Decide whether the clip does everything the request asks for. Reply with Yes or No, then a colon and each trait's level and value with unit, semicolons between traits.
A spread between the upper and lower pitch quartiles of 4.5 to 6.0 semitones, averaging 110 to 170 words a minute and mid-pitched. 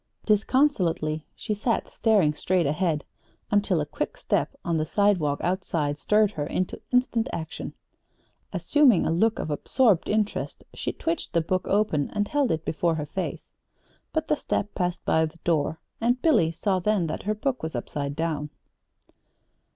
Yes: average, 5.2 semitones; average, 160 wpm; medium, 180 Hz